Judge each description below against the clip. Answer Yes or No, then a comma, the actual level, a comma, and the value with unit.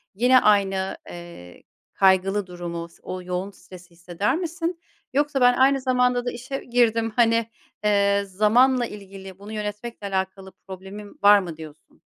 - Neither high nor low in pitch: No, high, 205 Hz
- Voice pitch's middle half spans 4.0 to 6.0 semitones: Yes, average, 4.5 semitones